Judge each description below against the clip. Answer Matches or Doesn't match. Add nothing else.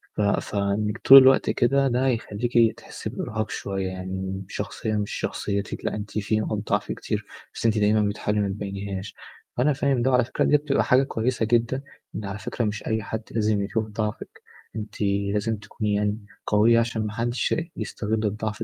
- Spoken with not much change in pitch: Matches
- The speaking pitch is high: Doesn't match